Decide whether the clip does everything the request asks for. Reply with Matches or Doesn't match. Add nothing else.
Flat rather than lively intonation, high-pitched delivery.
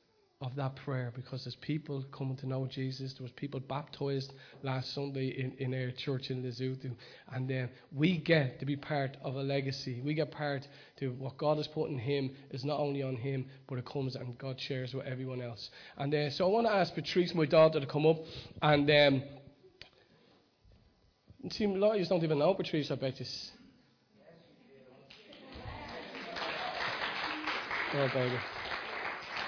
Doesn't match